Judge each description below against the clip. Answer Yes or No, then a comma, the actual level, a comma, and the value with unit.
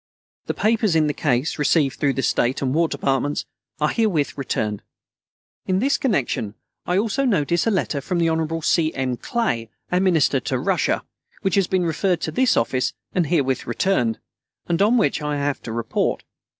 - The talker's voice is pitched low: No, medium, 160 Hz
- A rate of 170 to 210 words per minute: Yes, average, 180 wpm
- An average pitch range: No, wide, 5.8 semitones